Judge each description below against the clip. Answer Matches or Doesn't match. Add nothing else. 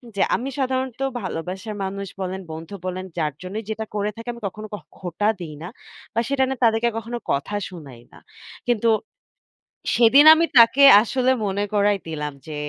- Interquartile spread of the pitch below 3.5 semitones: Doesn't match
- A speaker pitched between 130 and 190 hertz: Doesn't match